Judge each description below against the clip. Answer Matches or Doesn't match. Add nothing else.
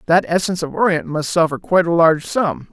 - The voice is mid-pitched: Matches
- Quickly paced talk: Matches